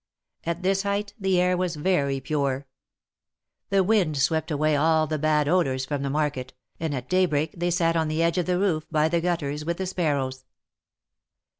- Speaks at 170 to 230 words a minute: Yes, average, 185 wpm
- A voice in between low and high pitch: Yes, medium, 160 Hz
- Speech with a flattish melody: No, average, 3.5 semitones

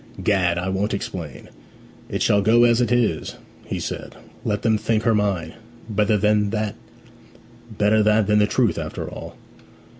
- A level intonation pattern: Yes, narrow, 1.7 semitones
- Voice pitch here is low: Yes, low, 105 Hz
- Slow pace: No, average, 145 wpm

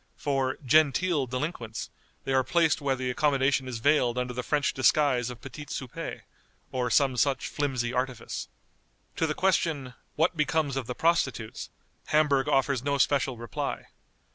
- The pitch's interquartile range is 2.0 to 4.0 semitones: Yes, average, 2.9 semitones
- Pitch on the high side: No, low, 135 Hz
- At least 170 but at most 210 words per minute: No, average, 150 wpm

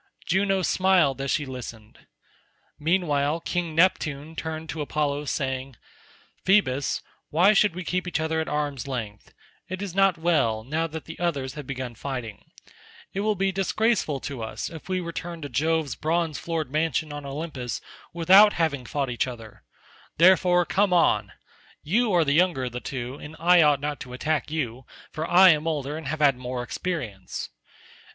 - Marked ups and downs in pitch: No, average, 4.5 semitones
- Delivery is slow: No, average, 170 wpm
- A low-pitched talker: No, medium, 155 Hz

